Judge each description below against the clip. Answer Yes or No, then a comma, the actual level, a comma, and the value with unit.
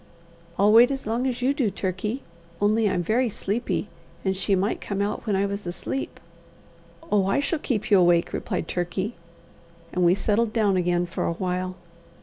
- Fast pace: No, average, 180 wpm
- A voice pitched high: Yes, high, 200 Hz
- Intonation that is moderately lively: Yes, average, 3.6 semitones